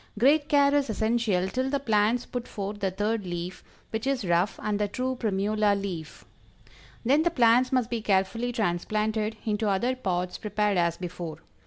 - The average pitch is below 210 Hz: No, high, 215 Hz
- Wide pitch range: No, average, 4.2 semitones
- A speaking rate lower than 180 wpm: Yes, average, 170 wpm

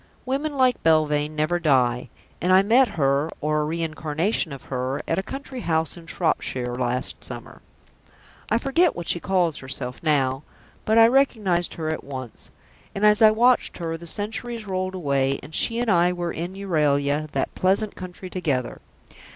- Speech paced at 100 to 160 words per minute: No, average, 170 wpm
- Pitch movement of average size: No, wide, 5.8 semitones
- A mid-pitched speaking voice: Yes, medium, 170 Hz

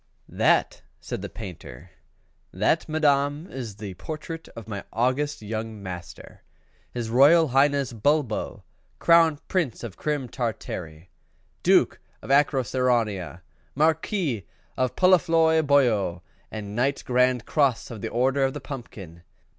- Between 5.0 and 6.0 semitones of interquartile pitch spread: Yes, average, 5.3 semitones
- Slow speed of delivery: Yes, slow, 120 wpm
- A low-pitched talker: Yes, low, 130 Hz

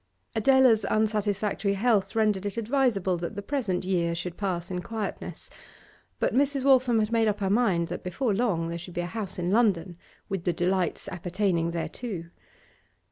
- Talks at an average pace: Yes, average, 170 wpm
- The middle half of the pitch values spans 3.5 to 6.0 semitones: Yes, average, 4.1 semitones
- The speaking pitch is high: Yes, high, 200 Hz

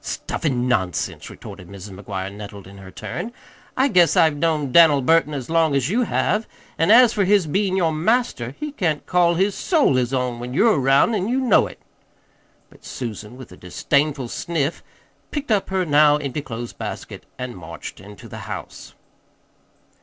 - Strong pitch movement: Yes, wide, 7.6 semitones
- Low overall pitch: No, medium, 150 Hz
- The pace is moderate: Yes, average, 180 wpm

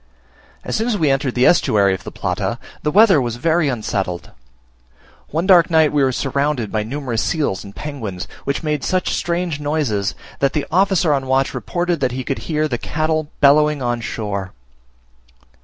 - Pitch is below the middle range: No, medium, 145 Hz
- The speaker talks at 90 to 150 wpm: No, average, 175 wpm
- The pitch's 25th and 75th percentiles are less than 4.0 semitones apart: No, average, 4.8 semitones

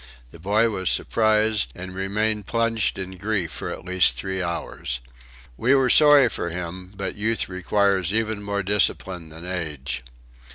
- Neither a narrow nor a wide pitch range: Yes, average, 3.3 semitones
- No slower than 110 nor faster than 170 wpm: Yes, average, 155 wpm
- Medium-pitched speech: No, very low, 95 Hz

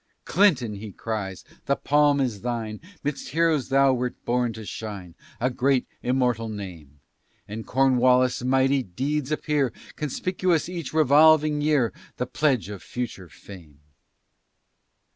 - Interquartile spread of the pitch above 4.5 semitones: Yes, average, 5.0 semitones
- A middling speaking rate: No, slow, 125 wpm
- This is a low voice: Yes, low, 125 Hz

